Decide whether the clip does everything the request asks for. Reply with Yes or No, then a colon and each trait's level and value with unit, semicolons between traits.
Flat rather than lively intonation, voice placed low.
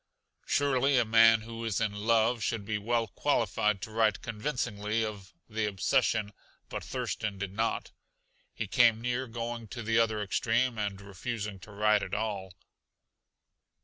Yes: narrow, 2.1 semitones; low, 110 Hz